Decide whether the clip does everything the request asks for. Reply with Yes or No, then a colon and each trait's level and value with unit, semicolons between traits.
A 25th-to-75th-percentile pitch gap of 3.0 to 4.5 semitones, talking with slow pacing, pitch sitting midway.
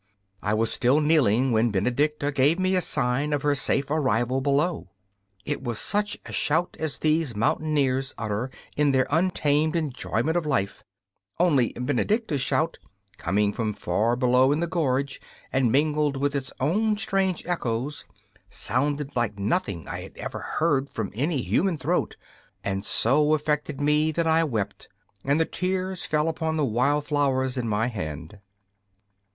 No: average, 4.2 semitones; average, 155 wpm; medium, 145 Hz